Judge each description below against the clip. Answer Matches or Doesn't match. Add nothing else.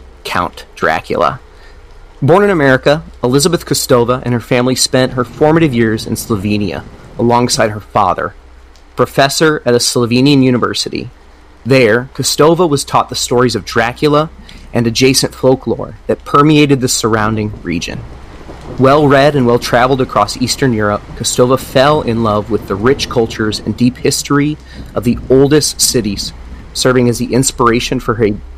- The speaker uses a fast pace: Doesn't match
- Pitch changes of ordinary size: Matches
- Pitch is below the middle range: Matches